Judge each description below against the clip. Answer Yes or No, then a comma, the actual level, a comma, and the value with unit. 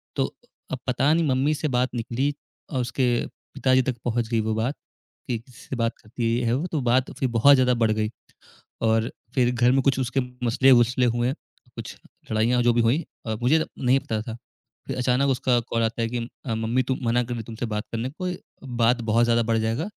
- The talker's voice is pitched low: Yes, low, 120 Hz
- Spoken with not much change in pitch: Yes, narrow, 2.2 semitones